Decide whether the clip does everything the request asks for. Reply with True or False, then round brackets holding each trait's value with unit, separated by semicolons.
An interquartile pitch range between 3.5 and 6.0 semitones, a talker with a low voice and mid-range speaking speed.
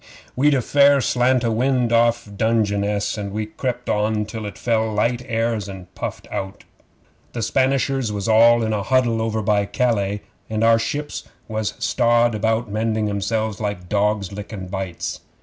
False (2.4 semitones; 110 Hz; 165 wpm)